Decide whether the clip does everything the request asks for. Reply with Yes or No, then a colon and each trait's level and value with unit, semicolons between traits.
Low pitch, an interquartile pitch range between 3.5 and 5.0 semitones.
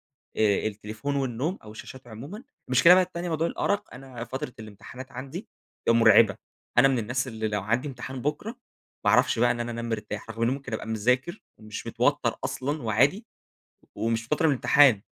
Yes: low, 125 Hz; average, 4.0 semitones